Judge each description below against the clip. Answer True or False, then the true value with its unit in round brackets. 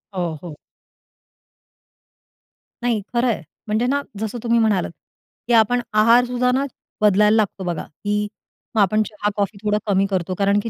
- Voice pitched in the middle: False (210 Hz)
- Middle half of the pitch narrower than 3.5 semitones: True (2.8 semitones)